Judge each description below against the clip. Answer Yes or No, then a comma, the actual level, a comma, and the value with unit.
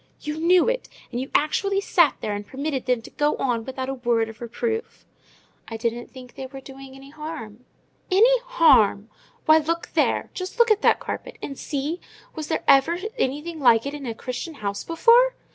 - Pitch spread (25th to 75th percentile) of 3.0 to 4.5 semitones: No, wide, 5.4 semitones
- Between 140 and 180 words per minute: No, average, 190 wpm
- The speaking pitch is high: Yes, very high, 275 Hz